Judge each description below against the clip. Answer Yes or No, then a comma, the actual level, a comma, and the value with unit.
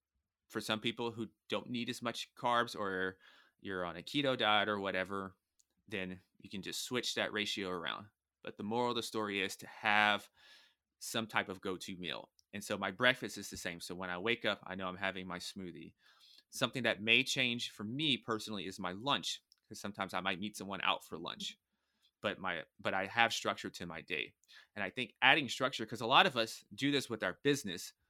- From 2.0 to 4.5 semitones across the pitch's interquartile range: Yes, average, 3.7 semitones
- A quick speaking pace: Yes, fast, 215 wpm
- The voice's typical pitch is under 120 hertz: Yes, low, 105 Hz